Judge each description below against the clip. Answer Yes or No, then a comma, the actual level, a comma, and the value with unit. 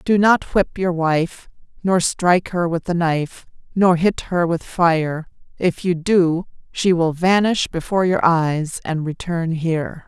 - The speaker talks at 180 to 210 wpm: No, average, 165 wpm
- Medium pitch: Yes, medium, 170 Hz